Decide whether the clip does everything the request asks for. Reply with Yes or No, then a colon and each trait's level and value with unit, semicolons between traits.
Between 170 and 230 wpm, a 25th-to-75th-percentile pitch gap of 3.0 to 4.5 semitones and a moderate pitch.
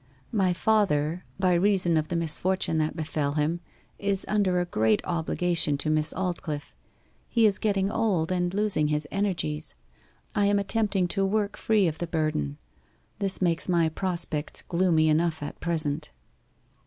No: average, 155 wpm; average, 3.9 semitones; medium, 175 Hz